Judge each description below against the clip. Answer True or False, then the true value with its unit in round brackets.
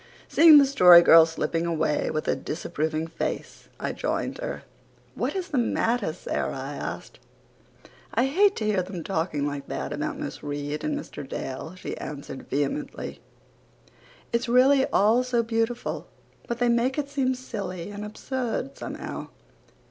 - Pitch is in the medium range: False (220 Hz)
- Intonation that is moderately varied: False (8.1 semitones)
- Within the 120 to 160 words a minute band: True (155 wpm)